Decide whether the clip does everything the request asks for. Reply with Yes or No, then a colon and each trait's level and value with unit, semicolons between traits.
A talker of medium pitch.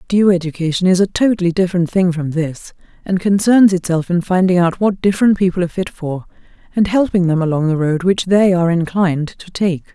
Yes: medium, 180 Hz